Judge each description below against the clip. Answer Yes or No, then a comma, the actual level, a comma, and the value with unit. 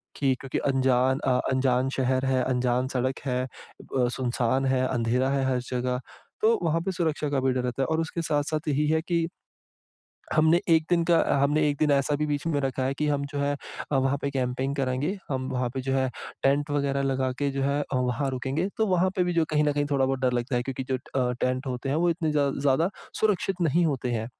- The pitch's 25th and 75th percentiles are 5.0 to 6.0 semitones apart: No, average, 2.7 semitones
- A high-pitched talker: No, low, 135 Hz